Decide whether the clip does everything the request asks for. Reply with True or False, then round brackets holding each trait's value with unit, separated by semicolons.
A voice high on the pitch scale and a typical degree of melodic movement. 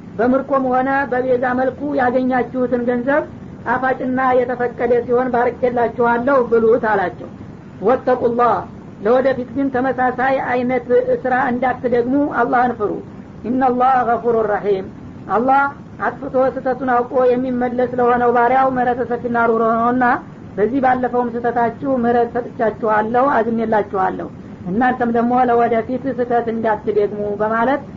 False (245 Hz; 1.5 semitones)